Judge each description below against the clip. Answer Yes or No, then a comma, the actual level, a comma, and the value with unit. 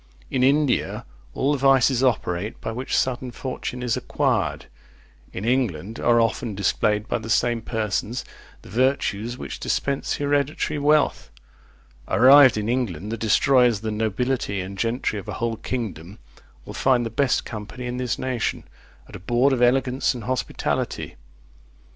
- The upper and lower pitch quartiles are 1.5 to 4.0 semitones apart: Yes, average, 3.2 semitones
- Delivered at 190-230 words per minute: No, average, 155 wpm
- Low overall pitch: Yes, low, 120 Hz